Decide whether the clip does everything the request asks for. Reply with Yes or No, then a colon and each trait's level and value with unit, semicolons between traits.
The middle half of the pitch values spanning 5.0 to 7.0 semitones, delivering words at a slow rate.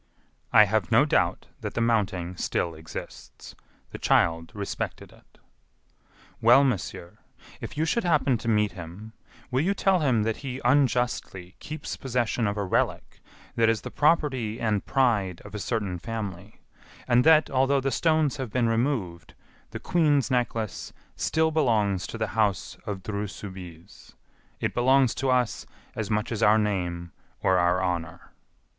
No: average, 5.3 semitones; average, 155 wpm